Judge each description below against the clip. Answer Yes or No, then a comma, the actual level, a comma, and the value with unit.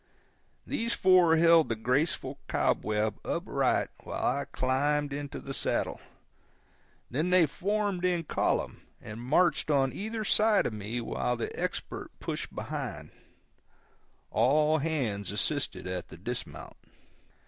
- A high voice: No, medium, 145 Hz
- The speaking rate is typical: No, slow, 125 wpm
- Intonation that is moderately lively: No, wide, 6.5 semitones